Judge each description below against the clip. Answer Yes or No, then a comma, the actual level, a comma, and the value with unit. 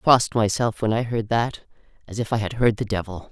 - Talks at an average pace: No, fast, 255 wpm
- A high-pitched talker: No, low, 110 Hz